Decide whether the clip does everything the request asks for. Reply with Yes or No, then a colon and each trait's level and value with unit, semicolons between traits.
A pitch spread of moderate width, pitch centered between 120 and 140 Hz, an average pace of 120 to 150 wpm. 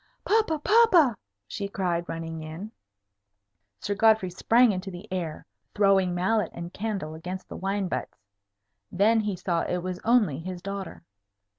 No: average, 3.6 semitones; high, 190 Hz; average, 145 wpm